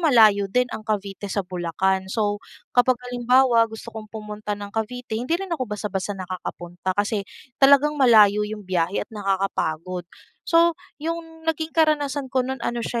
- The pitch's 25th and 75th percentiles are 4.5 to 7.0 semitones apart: Yes, average, 4.9 semitones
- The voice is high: Yes, high, 220 Hz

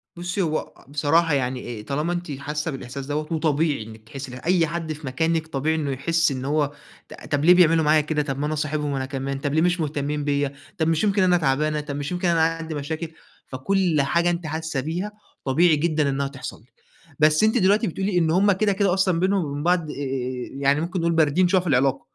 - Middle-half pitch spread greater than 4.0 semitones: No, average, 3.4 semitones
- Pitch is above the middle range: No, medium, 155 Hz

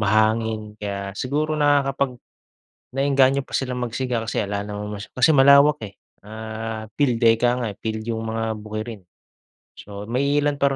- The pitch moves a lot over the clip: No, average, 4.1 semitones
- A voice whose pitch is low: Yes, low, 115 Hz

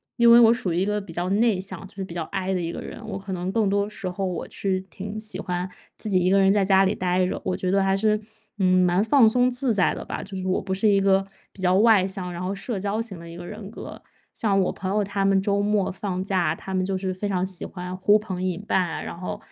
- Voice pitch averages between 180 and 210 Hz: Yes, high, 195 Hz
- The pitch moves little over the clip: Yes, narrow, 2.0 semitones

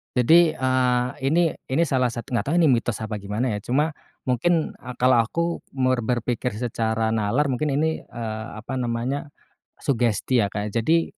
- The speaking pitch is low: Yes, low, 125 Hz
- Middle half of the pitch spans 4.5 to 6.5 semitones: No, average, 3.5 semitones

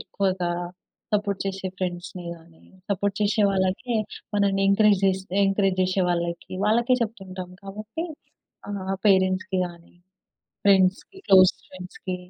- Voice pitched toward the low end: No, high, 190 Hz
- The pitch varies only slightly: Yes, narrow, 1.5 semitones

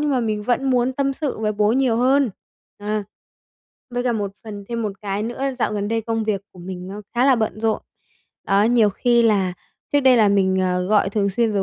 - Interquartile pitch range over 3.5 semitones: No, average, 3.2 semitones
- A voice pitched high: Yes, high, 220 Hz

